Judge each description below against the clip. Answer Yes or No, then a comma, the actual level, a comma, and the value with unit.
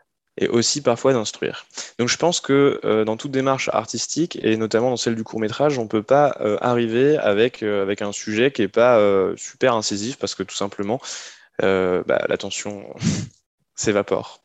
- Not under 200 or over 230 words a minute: No, average, 185 wpm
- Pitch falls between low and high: No, low, 115 Hz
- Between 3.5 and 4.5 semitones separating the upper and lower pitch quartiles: Yes, average, 3.9 semitones